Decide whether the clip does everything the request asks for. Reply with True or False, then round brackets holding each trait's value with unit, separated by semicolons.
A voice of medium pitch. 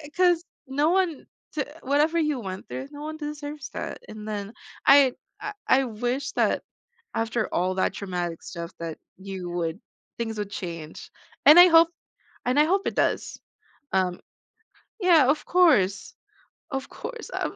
False (260 Hz)